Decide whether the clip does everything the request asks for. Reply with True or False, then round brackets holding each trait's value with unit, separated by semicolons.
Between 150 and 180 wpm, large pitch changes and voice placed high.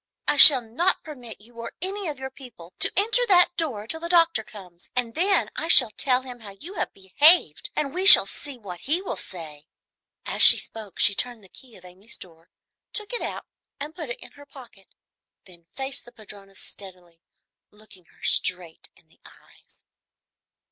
False (190 wpm; 8.1 semitones; 240 Hz)